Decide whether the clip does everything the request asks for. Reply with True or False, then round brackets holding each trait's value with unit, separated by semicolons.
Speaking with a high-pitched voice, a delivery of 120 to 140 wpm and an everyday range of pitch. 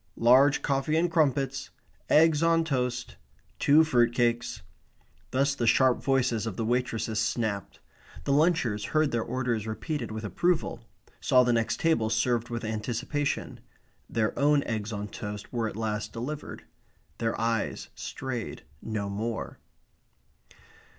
False (120 Hz; 135 wpm; 4.1 semitones)